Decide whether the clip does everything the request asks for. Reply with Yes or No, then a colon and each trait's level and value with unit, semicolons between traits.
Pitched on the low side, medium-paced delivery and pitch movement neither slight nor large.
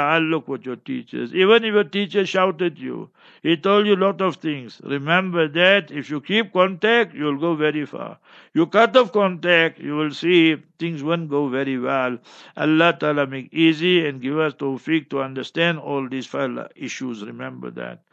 No: medium, 160 Hz; average, 180 wpm; average, 4.7 semitones